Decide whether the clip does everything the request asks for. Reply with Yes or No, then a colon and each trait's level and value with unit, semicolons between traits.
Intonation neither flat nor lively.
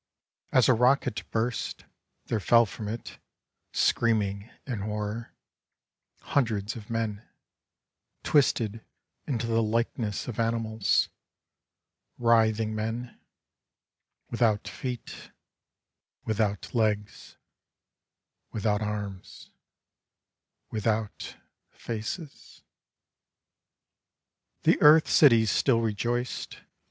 No: narrow, 1.9 semitones